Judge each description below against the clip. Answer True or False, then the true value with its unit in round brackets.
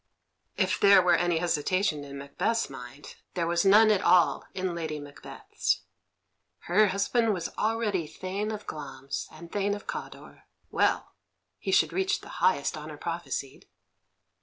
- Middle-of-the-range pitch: True (180 Hz)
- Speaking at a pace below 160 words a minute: True (145 wpm)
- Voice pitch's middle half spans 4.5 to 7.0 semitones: True (5.0 semitones)